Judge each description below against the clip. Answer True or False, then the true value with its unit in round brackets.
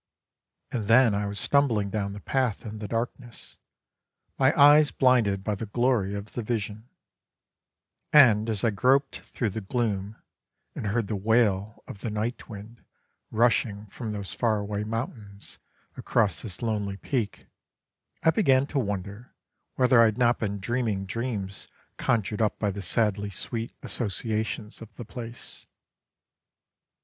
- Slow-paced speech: False (145 wpm)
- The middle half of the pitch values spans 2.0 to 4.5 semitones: True (2.9 semitones)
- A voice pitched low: True (110 Hz)